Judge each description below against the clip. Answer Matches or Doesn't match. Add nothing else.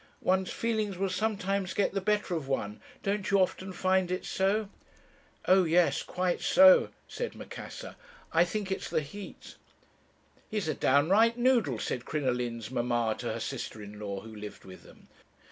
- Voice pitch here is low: Doesn't match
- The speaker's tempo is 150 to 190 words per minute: Matches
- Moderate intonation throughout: Doesn't match